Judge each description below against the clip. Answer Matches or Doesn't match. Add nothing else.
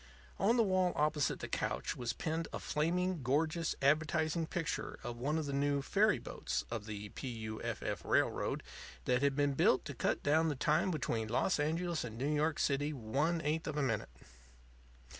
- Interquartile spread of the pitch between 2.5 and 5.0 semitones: Matches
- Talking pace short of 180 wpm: Doesn't match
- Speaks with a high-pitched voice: Doesn't match